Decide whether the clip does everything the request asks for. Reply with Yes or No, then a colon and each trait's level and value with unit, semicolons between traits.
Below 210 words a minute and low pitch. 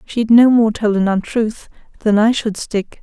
No: average, 200 wpm; high, 220 Hz